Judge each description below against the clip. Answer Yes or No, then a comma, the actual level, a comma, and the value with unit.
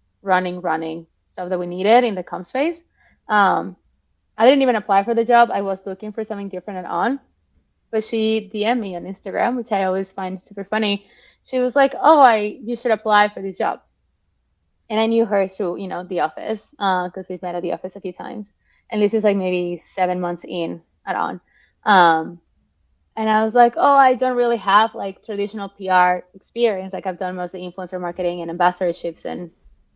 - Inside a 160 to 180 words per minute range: No, fast, 205 wpm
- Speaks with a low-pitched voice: No, high, 195 Hz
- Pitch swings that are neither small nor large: Yes, average, 3.6 semitones